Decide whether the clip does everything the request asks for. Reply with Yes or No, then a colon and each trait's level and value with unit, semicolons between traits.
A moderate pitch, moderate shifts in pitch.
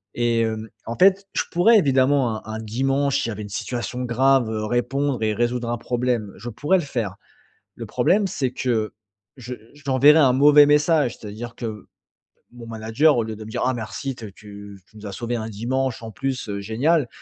No: low, 120 Hz; average, 3.7 semitones